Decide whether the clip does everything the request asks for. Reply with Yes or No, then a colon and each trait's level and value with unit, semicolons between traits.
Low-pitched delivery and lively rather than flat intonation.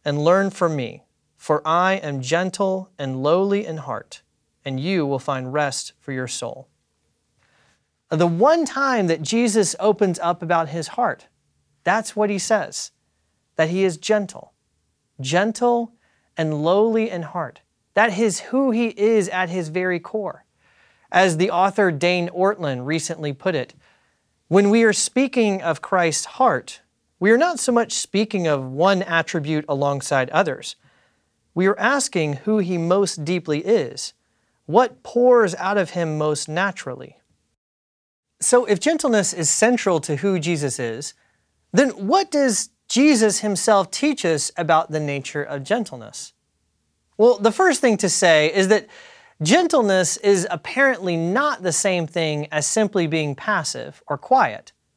No: medium, 185 Hz; wide, 5.9 semitones